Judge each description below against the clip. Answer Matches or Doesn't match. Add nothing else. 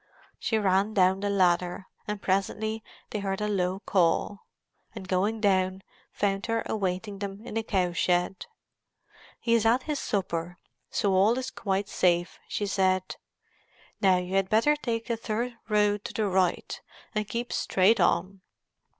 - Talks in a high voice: Matches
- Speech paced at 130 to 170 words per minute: Matches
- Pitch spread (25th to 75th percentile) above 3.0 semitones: Doesn't match